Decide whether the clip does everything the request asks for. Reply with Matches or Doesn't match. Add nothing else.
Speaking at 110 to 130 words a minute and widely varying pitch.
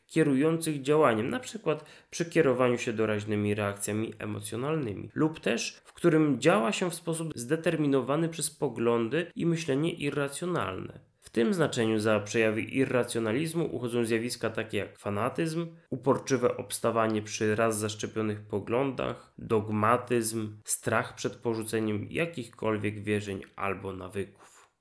Matches